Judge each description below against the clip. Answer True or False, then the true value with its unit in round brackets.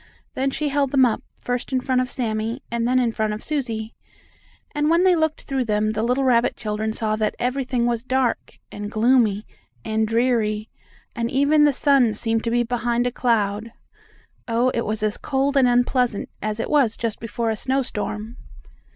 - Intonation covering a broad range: False (3.1 semitones)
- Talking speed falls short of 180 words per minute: False (185 wpm)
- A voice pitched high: True (240 Hz)